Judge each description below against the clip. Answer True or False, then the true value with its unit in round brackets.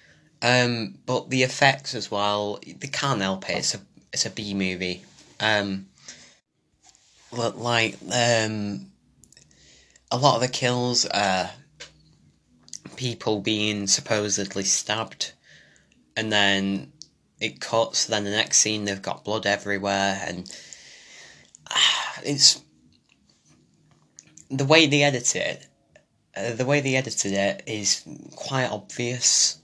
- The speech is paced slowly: True (120 wpm)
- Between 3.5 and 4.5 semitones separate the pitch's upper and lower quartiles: True (3.8 semitones)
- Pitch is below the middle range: True (105 Hz)